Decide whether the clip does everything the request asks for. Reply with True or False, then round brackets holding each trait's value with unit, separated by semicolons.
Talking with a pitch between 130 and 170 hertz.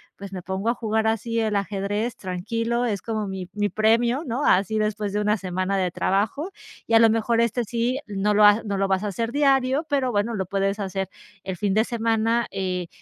False (215 Hz)